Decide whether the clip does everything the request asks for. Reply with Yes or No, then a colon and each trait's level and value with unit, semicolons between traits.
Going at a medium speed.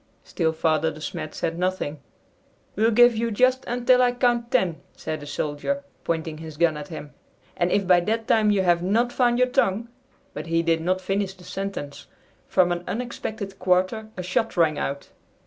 Yes: average, 190 wpm